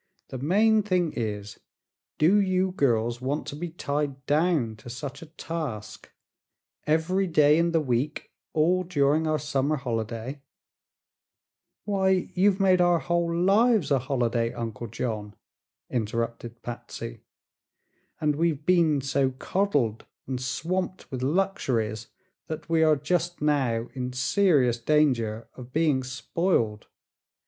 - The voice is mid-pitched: Yes, medium, 145 Hz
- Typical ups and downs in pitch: No, wide, 6.0 semitones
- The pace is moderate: No, slow, 130 wpm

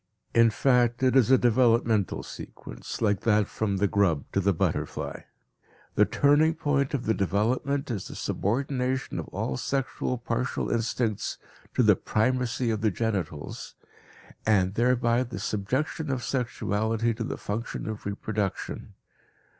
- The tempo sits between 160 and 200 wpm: No, average, 140 wpm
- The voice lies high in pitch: No, low, 115 Hz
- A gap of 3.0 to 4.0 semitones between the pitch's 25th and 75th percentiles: Yes, average, 3.6 semitones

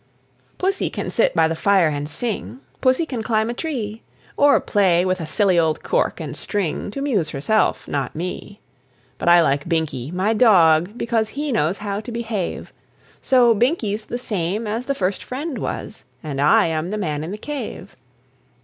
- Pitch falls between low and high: No, high, 205 Hz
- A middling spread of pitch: No, wide, 6.0 semitones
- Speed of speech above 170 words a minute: Yes, average, 180 wpm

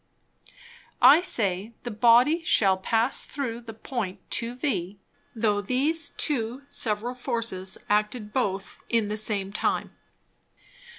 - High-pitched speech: Yes, high, 225 Hz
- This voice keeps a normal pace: No, slow, 120 wpm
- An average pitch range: Yes, average, 3.4 semitones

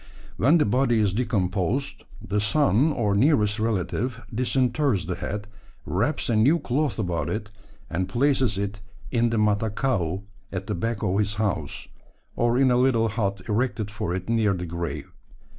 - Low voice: Yes, low, 110 Hz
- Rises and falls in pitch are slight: No, average, 3.8 semitones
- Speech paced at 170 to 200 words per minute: No, average, 160 wpm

